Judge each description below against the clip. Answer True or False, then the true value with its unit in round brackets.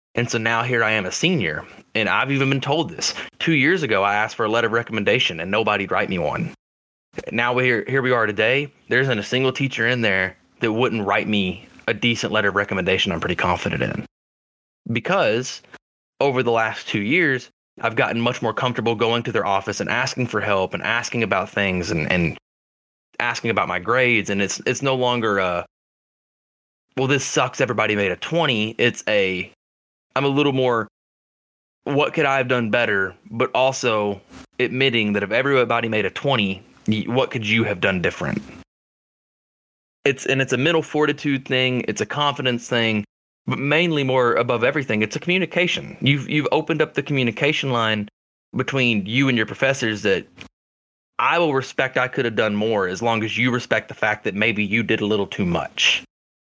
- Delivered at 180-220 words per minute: True (190 wpm)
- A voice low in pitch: True (120 Hz)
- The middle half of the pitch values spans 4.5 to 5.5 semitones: False (4.1 semitones)